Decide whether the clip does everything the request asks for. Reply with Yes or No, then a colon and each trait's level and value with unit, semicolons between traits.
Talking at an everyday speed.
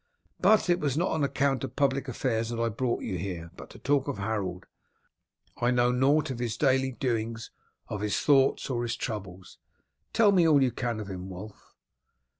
Yes: average, 195 wpm